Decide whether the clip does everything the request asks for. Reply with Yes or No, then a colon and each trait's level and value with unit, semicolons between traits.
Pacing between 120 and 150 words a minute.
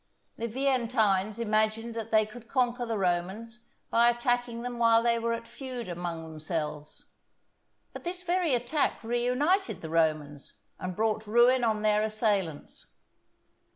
Yes: average, 140 wpm